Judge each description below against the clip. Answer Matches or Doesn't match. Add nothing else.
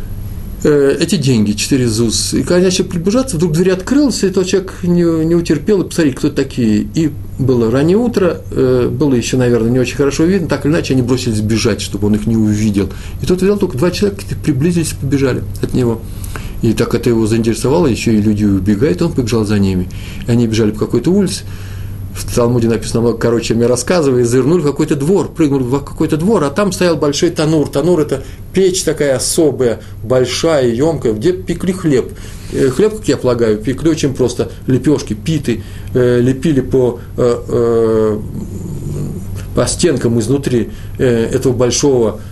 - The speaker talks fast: Matches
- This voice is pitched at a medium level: Doesn't match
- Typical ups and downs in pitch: Doesn't match